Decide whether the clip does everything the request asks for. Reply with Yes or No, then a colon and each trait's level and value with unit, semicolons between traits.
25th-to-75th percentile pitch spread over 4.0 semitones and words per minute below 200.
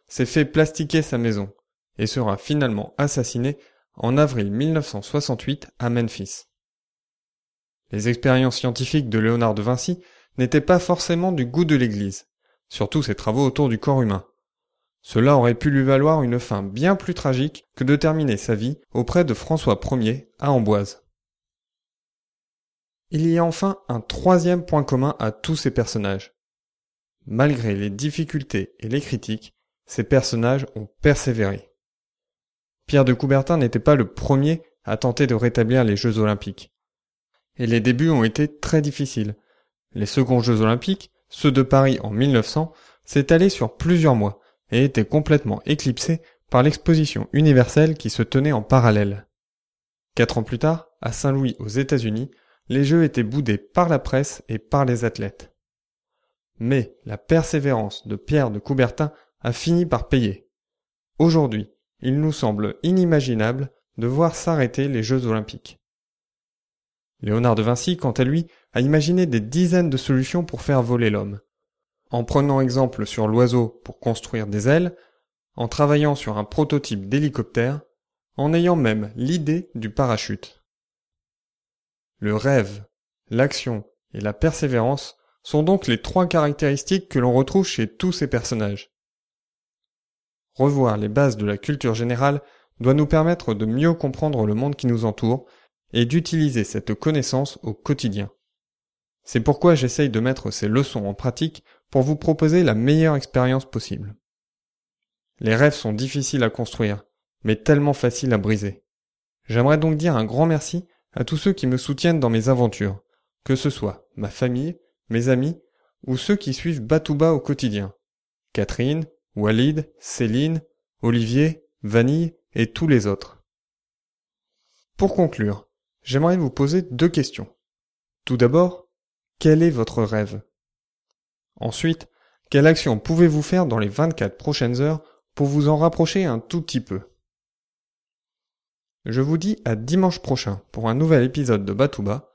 Yes: average, 5.3 semitones; average, 150 wpm